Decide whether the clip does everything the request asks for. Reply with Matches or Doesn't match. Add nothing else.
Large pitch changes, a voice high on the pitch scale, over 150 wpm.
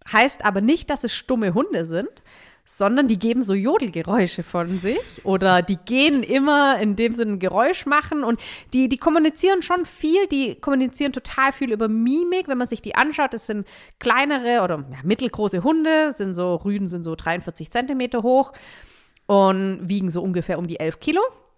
Matches